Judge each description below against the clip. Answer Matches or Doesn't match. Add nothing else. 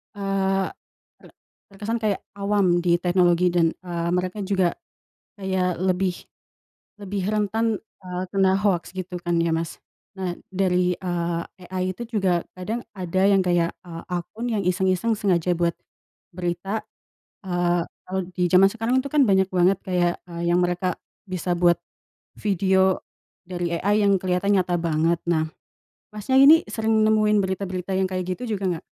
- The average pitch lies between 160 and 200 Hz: Matches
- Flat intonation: Matches